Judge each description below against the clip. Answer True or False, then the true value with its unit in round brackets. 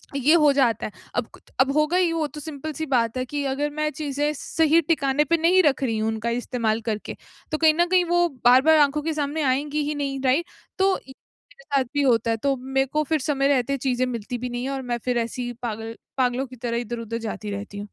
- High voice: True (270 Hz)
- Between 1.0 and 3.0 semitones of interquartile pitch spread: False (4.0 semitones)